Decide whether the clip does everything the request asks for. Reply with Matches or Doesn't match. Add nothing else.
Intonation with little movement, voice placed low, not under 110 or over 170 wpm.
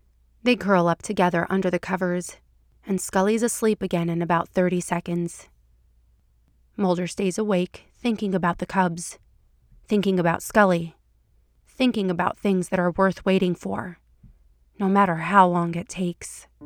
Doesn't match